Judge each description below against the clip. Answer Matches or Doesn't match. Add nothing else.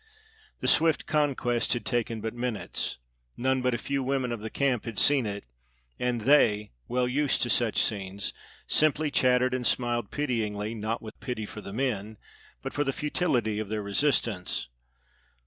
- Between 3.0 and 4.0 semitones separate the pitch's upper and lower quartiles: Matches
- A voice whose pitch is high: Doesn't match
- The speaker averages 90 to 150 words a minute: Doesn't match